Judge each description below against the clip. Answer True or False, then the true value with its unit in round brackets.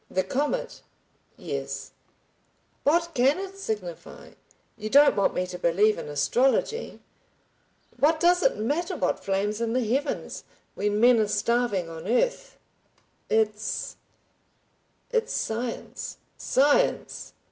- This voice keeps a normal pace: False (110 wpm)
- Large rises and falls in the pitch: True (6.3 semitones)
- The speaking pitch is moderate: False (235 Hz)